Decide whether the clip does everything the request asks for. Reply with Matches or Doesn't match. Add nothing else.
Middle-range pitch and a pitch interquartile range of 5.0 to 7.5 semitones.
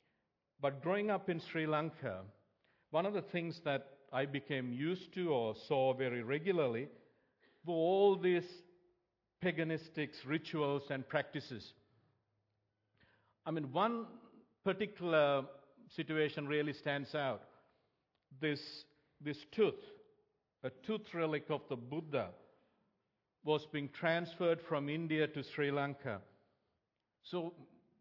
Doesn't match